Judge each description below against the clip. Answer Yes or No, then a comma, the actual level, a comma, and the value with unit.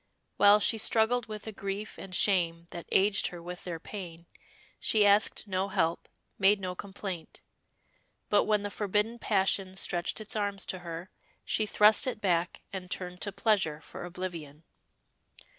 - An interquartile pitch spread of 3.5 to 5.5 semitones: No, average, 2.8 semitones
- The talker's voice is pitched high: Yes, high, 195 Hz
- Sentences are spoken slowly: No, average, 160 wpm